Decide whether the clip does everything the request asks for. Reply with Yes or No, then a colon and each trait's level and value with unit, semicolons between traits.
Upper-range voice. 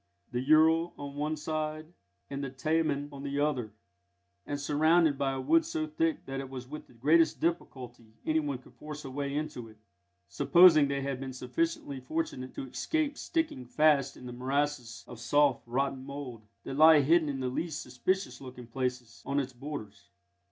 No: medium, 140 Hz